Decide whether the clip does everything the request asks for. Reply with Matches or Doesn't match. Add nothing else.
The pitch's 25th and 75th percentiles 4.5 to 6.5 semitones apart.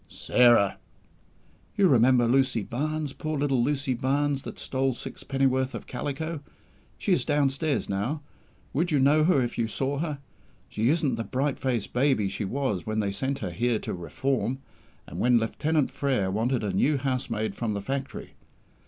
Doesn't match